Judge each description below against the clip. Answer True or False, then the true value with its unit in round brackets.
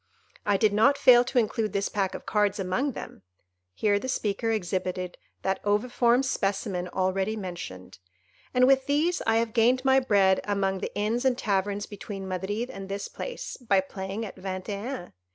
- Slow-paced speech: False (170 wpm)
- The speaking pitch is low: False (205 Hz)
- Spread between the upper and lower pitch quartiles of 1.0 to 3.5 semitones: False (4.1 semitones)